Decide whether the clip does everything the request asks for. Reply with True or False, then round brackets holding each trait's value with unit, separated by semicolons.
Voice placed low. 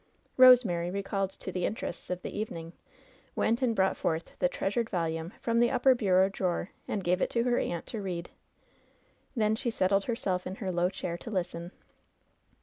False (190 Hz)